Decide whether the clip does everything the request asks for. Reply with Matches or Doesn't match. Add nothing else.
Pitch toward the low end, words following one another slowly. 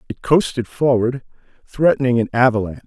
Matches